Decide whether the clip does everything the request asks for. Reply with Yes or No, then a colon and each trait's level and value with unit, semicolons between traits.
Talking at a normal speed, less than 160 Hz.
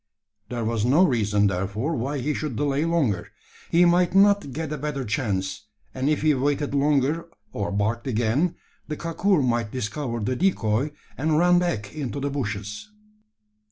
Yes: average, 160 wpm; low, 135 Hz